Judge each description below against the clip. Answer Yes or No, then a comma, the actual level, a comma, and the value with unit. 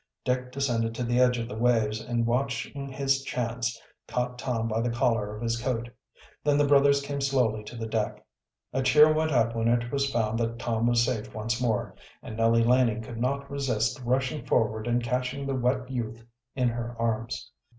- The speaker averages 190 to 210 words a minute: Yes, average, 195 wpm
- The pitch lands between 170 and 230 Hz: No, low, 120 Hz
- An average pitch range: No, narrow, 2.3 semitones